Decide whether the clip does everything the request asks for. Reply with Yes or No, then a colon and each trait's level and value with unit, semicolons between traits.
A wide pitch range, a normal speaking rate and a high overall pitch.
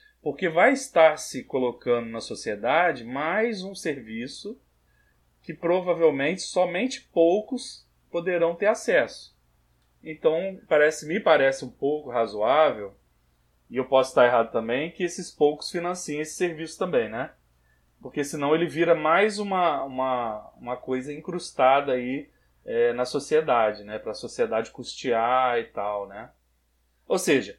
No: wide, 6.8 semitones; average, 135 wpm; medium, 155 Hz